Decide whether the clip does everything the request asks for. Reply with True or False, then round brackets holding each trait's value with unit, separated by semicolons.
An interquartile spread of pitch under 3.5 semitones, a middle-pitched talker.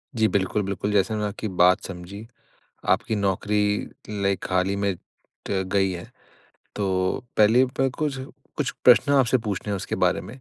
False (2.5 semitones; 100 Hz)